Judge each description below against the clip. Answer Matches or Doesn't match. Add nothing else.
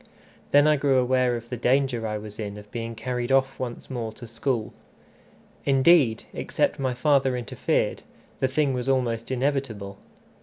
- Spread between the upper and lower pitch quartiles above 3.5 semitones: Doesn't match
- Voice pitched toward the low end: Matches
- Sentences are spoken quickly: Doesn't match